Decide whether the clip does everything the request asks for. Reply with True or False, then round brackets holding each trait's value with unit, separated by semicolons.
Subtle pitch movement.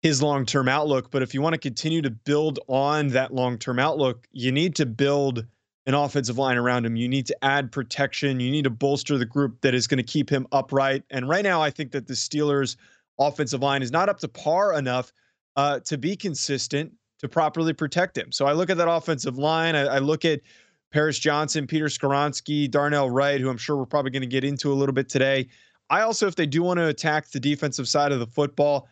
True (2.2 semitones)